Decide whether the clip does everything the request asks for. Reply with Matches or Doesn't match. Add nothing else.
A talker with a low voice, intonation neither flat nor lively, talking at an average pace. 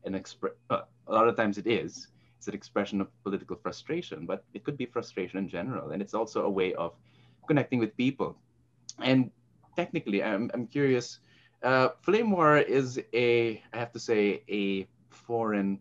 Matches